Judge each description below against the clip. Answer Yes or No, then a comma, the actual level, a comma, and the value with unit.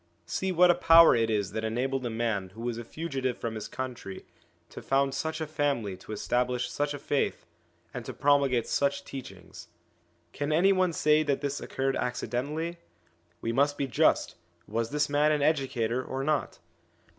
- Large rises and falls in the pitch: No, average, 4.0 semitones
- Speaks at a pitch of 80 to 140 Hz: Yes, low, 135 Hz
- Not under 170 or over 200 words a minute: Yes, average, 180 wpm